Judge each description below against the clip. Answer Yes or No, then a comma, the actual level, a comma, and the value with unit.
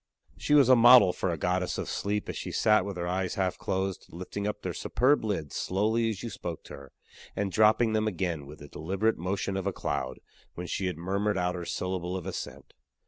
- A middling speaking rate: No, fast, 220 wpm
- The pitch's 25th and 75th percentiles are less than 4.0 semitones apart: Yes, average, 3.2 semitones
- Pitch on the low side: Yes, very low, 95 Hz